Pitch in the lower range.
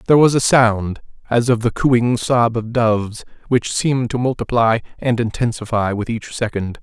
Yes: low, 115 Hz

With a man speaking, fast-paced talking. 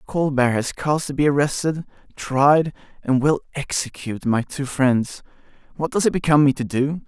No: male; average, 170 wpm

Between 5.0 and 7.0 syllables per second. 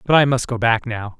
Yes: 5.6 syllables/s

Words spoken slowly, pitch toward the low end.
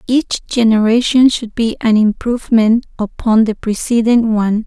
No: slow, 130 wpm; high, 225 Hz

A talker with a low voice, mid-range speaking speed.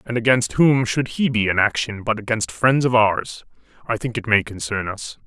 No: low, 110 Hz; fast, 215 wpm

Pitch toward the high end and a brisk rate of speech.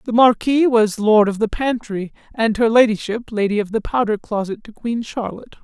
No: high, 220 Hz; average, 190 wpm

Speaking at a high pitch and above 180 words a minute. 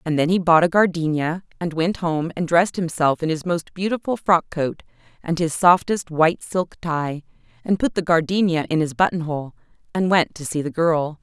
No: medium, 165 Hz; average, 200 wpm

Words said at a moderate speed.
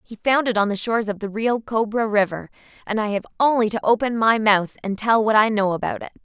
No: fast, 250 wpm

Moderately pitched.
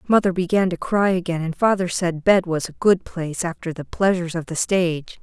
Yes: medium, 175 Hz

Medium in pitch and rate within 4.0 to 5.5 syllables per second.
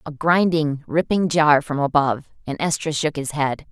Yes: medium, 150 Hz; 4.8 syllables/s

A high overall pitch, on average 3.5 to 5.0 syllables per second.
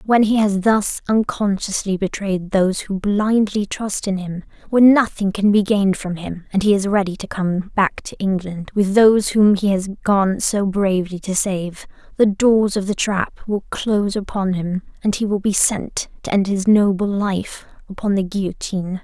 Yes: high, 200 Hz; 4.6 syllables/s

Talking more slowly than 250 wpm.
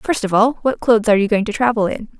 No: fast, 300 wpm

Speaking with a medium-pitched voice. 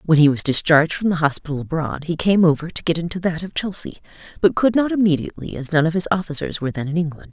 Yes: medium, 165 Hz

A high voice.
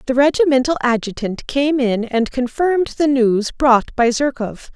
Yes: very high, 260 Hz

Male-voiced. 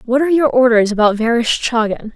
No: female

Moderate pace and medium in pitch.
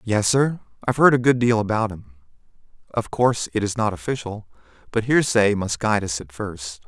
No: average, 185 wpm; low, 110 Hz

